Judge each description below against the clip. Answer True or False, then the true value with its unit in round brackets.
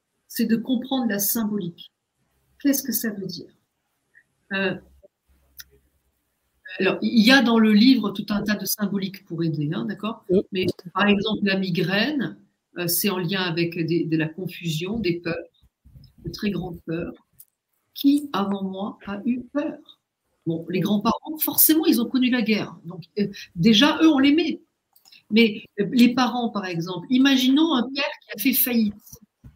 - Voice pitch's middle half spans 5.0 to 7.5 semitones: True (5.3 semitones)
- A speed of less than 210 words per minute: True (165 wpm)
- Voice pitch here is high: True (205 Hz)